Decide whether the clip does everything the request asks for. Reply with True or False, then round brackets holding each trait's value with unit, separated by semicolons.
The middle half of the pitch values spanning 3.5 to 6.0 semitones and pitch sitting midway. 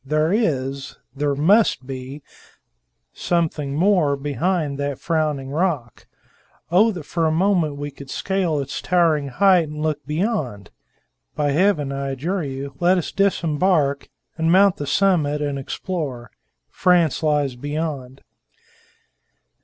True (4.1 semitones; 150 Hz)